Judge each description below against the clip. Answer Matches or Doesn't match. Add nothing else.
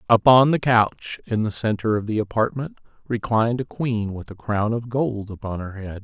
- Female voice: Doesn't match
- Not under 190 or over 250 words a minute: Matches